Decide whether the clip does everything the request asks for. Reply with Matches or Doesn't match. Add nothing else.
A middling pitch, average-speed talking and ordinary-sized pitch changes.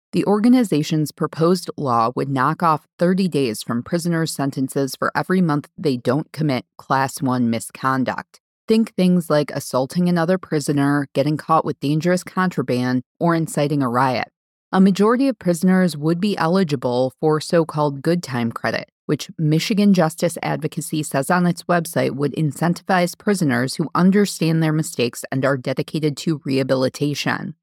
Matches